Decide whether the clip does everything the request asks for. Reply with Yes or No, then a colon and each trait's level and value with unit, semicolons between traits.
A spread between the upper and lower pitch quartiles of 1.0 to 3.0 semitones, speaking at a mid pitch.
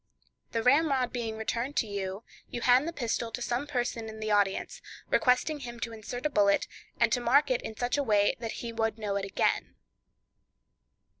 No: narrow, 2.5 semitones; high, 235 Hz